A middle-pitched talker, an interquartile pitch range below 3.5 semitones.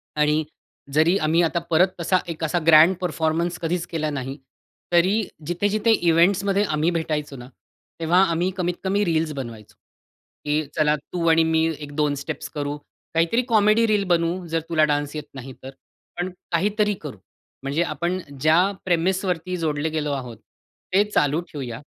Yes: medium, 165 Hz; average, 3.1 semitones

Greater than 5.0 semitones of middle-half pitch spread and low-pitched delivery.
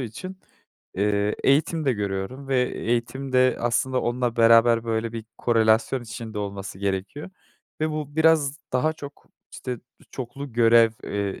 No: average, 3.6 semitones; low, 120 Hz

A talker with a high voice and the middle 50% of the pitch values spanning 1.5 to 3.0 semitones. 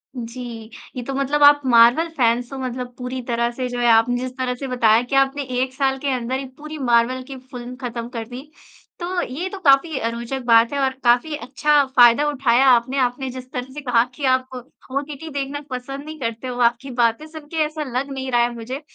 Yes: very high, 255 Hz; narrow, 2.4 semitones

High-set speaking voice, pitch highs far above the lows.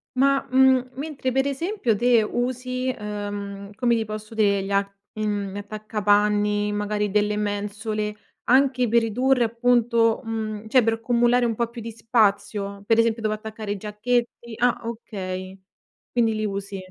No: high, 220 Hz; average, 2.7 semitones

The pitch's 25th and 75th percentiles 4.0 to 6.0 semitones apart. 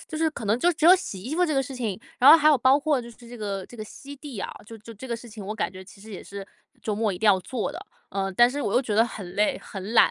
Yes: average, 4.9 semitones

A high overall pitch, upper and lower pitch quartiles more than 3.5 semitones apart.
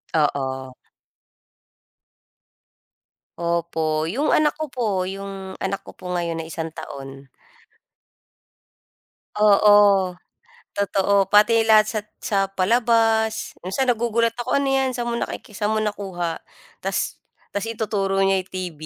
Yes: high, 200 Hz; average, 4.5 semitones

